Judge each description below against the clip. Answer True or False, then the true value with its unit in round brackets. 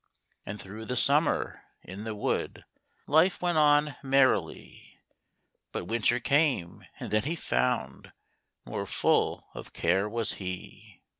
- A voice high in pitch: False (125 Hz)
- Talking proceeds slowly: True (130 wpm)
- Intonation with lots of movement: True (6.0 semitones)